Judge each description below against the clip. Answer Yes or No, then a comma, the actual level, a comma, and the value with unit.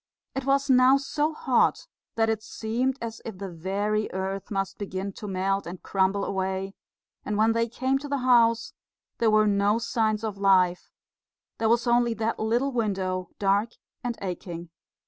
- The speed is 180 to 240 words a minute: No, average, 165 wpm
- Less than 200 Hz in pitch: No, high, 215 Hz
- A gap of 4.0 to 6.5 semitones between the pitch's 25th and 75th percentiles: No, average, 3.5 semitones